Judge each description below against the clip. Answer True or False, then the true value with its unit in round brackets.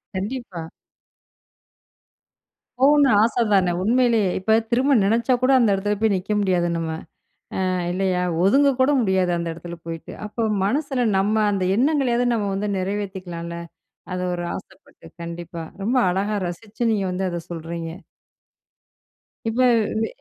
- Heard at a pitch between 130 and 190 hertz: False (200 Hz)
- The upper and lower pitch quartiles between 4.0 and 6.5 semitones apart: True (4.7 semitones)